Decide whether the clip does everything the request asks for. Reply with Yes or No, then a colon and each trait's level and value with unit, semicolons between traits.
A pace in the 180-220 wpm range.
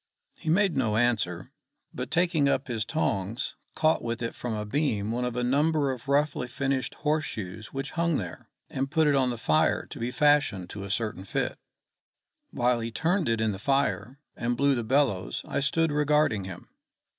Yes: average, 190 wpm